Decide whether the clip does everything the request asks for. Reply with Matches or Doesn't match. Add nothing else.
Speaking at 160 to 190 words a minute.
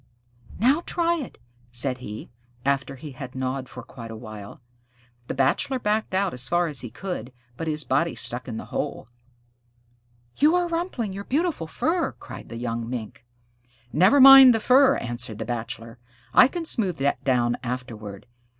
Matches